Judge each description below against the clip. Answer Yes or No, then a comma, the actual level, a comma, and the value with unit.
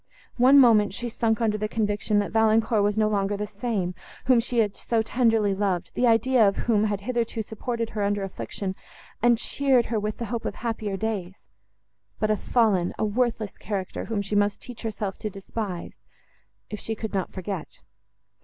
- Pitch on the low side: No, high, 215 Hz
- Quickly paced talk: No, average, 180 wpm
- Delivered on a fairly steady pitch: Yes, narrow, 2.2 semitones